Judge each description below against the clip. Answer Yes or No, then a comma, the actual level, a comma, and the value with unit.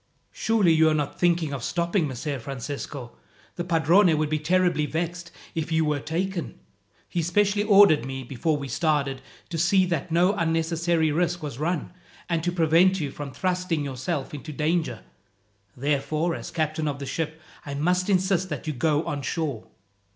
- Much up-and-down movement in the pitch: No, average, 3.1 semitones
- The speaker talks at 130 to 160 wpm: No, average, 170 wpm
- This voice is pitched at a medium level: Yes, medium, 160 Hz